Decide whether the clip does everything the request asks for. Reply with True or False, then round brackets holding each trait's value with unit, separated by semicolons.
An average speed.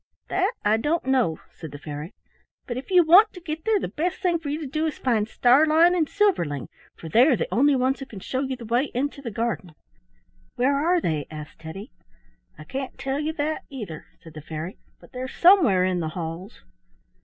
False (210 wpm)